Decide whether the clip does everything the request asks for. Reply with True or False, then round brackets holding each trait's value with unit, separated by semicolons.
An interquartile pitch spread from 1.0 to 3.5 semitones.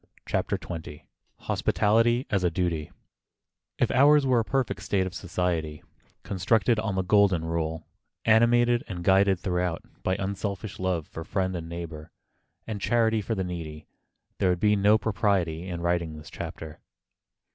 False (4.1 semitones)